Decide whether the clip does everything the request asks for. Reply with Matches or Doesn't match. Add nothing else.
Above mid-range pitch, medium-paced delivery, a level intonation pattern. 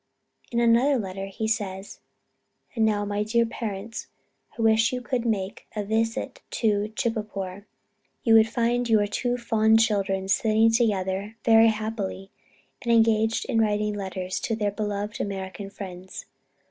Matches